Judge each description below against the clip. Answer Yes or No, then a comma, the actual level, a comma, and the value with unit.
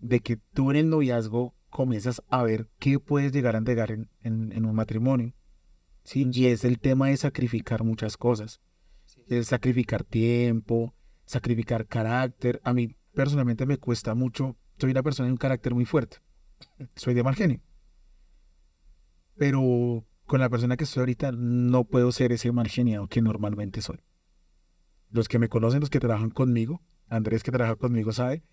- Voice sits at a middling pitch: No, low, 120 Hz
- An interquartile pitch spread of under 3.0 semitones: Yes, narrow, 2.4 semitones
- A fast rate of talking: No, average, 165 wpm